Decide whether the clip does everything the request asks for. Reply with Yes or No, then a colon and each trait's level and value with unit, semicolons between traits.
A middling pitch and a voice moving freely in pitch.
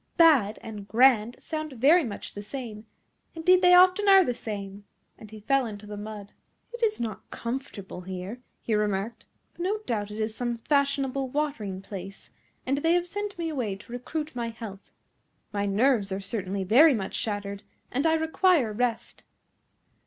No: high, 235 Hz; wide, 6.5 semitones